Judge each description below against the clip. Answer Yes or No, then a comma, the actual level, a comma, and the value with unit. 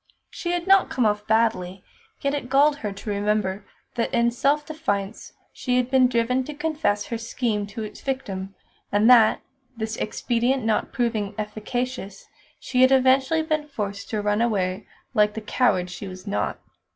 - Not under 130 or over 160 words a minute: No, average, 170 wpm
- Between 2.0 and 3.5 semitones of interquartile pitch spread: No, average, 4.1 semitones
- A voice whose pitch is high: Yes, high, 230 Hz